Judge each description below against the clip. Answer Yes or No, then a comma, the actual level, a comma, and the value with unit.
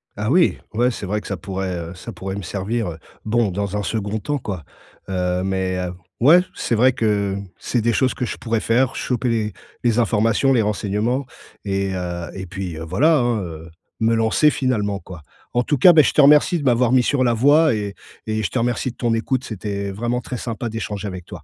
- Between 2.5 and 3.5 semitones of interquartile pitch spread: No, average, 4.0 semitones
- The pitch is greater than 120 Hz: No, low, 110 Hz